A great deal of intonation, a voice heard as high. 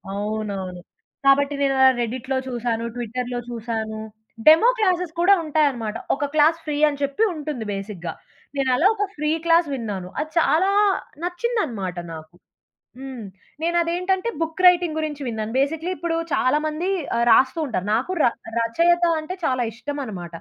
Yes: wide, 6.3 semitones; very high, 275 Hz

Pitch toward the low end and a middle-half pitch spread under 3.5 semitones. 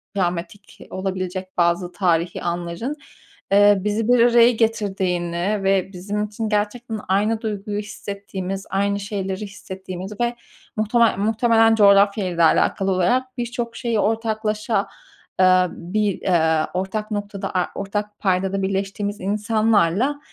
No: high, 200 Hz; narrow, 2.5 semitones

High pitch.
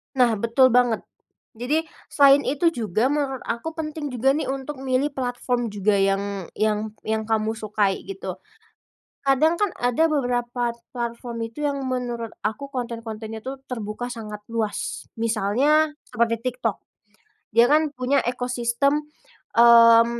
Yes: high, 245 Hz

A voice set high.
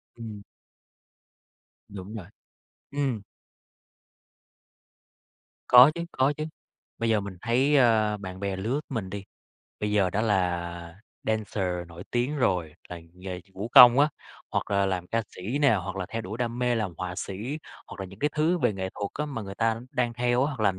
No: low, 105 Hz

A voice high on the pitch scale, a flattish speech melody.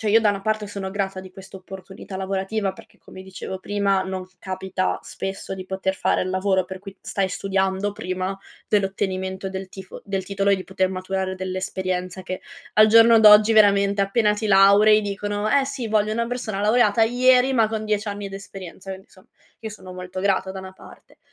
Yes: high, 195 Hz; narrow, 1.9 semitones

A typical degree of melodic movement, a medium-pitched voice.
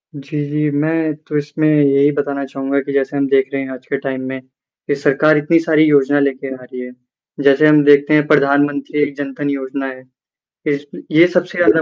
No: narrow, 1.7 semitones; medium, 145 Hz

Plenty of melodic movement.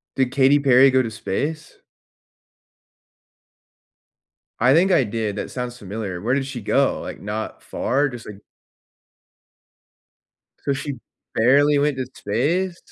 No: average, 4.3 semitones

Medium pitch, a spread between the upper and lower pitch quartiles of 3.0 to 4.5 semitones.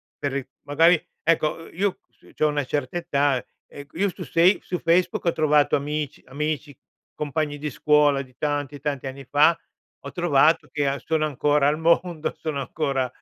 No: medium, 150 Hz; narrow, 2.4 semitones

